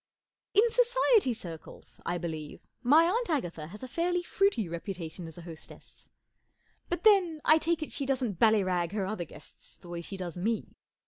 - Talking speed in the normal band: Yes, average, 180 wpm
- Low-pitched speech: No, high, 220 Hz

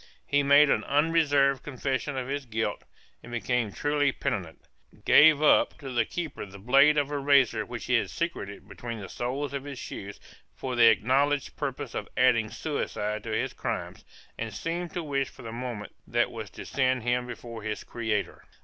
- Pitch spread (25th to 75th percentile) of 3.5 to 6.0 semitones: Yes, average, 4.1 semitones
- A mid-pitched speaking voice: No, low, 130 Hz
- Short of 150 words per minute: No, average, 185 wpm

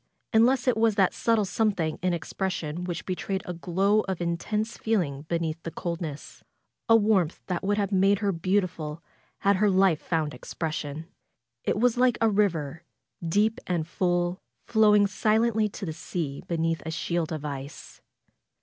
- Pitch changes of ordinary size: Yes, average, 4.2 semitones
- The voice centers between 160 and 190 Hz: Yes, medium, 185 Hz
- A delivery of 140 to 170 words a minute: Yes, average, 165 wpm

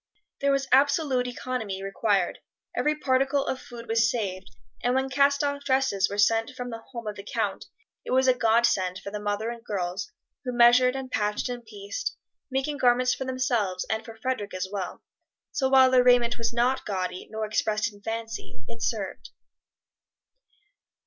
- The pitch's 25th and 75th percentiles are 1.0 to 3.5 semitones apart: No, average, 4.0 semitones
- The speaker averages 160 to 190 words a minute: Yes, average, 175 wpm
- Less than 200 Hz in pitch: No, high, 235 Hz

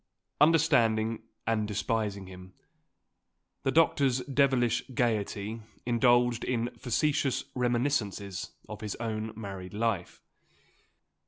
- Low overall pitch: Yes, low, 115 Hz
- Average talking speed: No, slow, 90 wpm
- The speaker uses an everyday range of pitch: Yes, average, 3.2 semitones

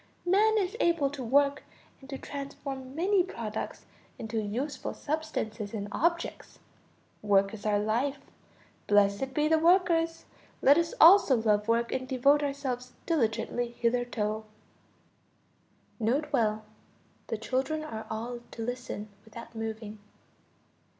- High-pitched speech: Yes, very high, 255 Hz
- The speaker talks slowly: Yes, slow, 120 wpm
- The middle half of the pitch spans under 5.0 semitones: No, average, 5.3 semitones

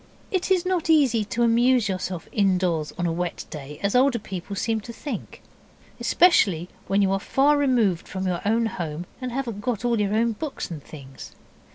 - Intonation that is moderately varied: No, wide, 5.7 semitones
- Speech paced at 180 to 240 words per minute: Yes, average, 190 wpm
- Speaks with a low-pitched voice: No, high, 210 Hz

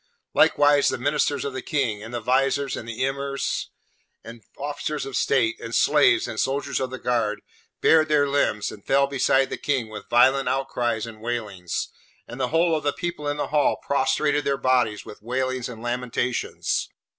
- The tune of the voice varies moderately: Yes, average, 3.1 semitones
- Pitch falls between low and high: No, low, 130 Hz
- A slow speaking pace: No, average, 180 wpm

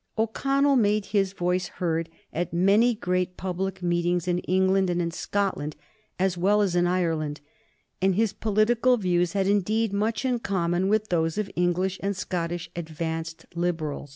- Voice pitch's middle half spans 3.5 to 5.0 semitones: No, average, 2.8 semitones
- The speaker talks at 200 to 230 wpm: No, average, 155 wpm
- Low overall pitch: No, medium, 185 Hz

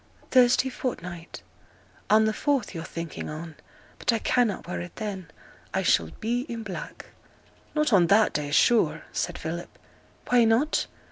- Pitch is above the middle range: Yes, high, 215 Hz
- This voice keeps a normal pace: Yes, average, 150 wpm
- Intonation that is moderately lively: No, wide, 5.9 semitones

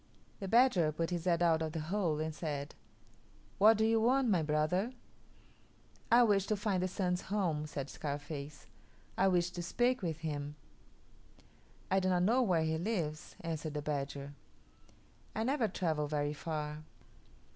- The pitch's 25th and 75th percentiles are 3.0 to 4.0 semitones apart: No, average, 4.6 semitones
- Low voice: No, medium, 170 Hz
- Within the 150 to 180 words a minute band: Yes, average, 160 wpm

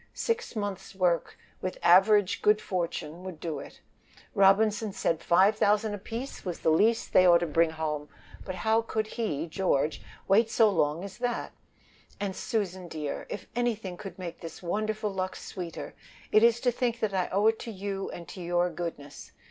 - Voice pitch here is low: No, high, 190 Hz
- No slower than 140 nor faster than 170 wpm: No, average, 185 wpm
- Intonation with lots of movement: No, average, 3.9 semitones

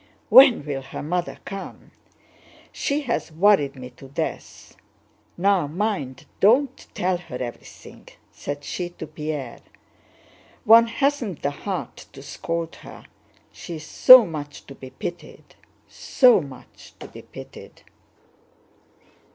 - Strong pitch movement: Yes, wide, 6.8 semitones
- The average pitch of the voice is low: No, medium, 170 Hz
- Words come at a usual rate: No, slow, 125 wpm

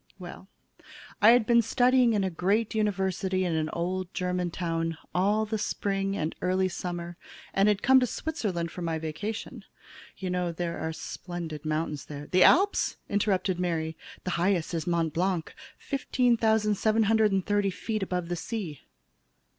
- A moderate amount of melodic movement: Yes, average, 3.8 semitones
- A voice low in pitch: No, medium, 185 Hz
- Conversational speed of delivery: Yes, average, 155 wpm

